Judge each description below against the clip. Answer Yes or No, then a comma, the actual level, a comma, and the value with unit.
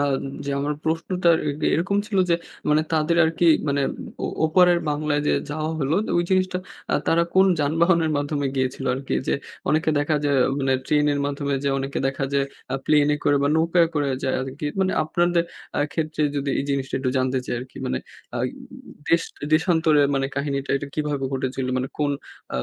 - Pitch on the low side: No, medium, 150 Hz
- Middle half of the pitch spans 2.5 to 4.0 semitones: Yes, average, 2.9 semitones